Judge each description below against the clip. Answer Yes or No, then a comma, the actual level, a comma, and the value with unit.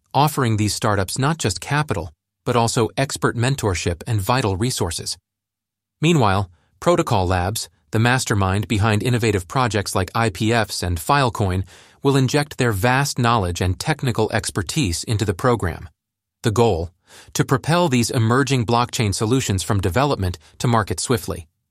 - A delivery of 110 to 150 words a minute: Yes, slow, 135 wpm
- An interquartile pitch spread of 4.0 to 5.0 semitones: Yes, average, 4.4 semitones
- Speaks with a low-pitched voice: Yes, low, 110 Hz